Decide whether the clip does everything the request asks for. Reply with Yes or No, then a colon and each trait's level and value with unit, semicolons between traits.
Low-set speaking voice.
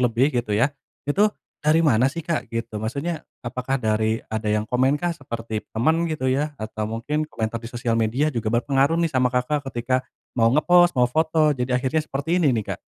Yes: low, 130 Hz